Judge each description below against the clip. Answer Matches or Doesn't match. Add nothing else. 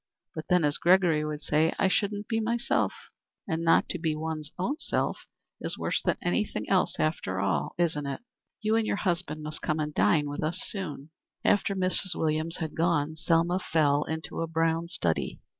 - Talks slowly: Doesn't match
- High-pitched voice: Doesn't match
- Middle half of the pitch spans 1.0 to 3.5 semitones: Matches